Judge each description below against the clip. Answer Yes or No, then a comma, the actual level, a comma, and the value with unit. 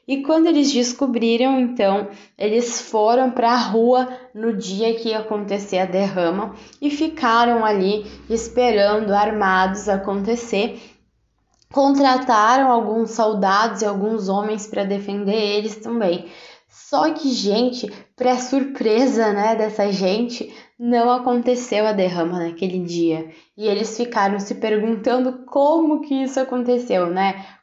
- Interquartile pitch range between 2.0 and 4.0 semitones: Yes, average, 3.5 semitones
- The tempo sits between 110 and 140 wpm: Yes, average, 125 wpm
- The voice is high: Yes, high, 225 Hz